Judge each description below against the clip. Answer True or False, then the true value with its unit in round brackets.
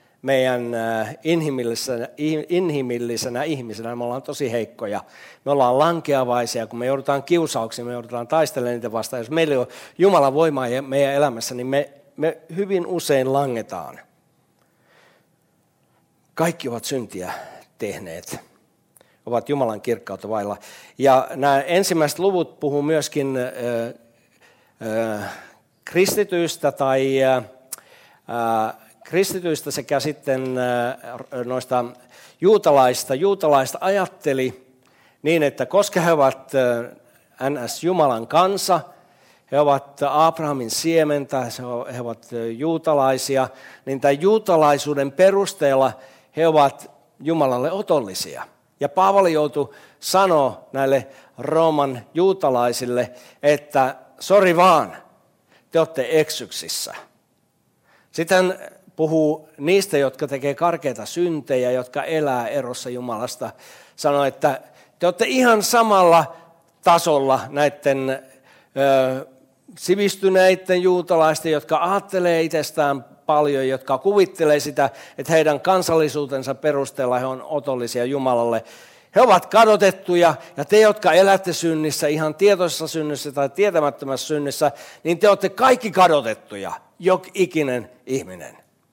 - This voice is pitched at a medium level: True (145 Hz)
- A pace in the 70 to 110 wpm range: True (105 wpm)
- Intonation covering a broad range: False (4.4 semitones)